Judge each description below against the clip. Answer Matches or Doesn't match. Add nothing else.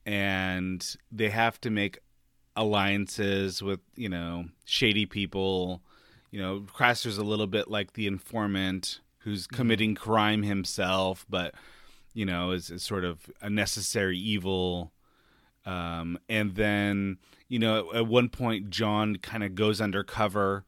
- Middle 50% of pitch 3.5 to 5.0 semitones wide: Doesn't match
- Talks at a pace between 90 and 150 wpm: Matches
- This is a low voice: Matches